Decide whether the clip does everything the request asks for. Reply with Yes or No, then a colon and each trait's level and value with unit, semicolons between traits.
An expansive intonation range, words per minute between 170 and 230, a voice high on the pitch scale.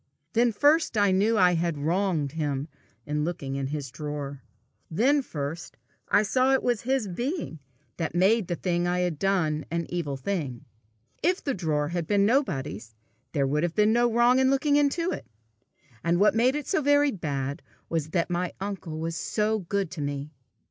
No: wide, 7.3 semitones; average, 185 wpm; medium, 175 Hz